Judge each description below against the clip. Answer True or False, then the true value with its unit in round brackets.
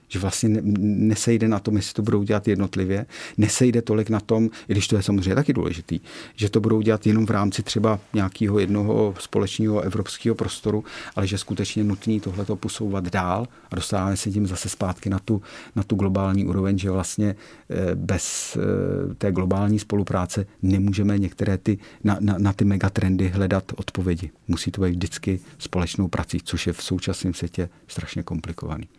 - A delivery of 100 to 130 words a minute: False (170 wpm)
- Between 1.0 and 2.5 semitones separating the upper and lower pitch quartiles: True (2.2 semitones)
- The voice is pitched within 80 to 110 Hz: True (100 Hz)